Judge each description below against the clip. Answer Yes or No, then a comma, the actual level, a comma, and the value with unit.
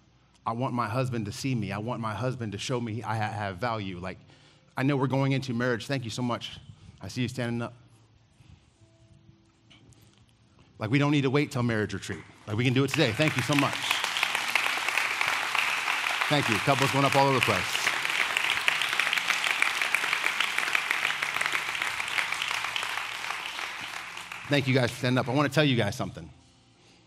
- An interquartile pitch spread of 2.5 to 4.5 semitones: Yes, average, 3.5 semitones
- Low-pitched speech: Yes, low, 120 Hz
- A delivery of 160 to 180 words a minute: Yes, average, 165 wpm